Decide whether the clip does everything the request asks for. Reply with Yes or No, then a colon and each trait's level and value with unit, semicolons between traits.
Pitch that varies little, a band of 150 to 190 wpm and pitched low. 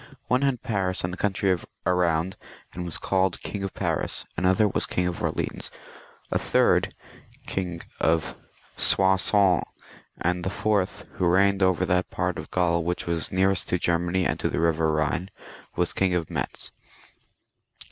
Yes: narrow, 1.9 semitones; average, 155 wpm; very low, 90 Hz